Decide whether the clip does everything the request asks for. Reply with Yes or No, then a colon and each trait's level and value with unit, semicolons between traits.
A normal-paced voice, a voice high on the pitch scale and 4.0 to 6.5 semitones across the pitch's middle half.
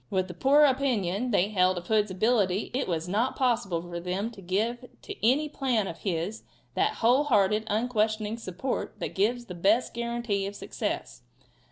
Yes: average, 175 wpm; high, 215 Hz; average, 4.4 semitones